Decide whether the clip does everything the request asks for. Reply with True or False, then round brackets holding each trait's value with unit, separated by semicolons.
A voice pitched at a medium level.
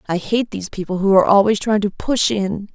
False (200 Hz)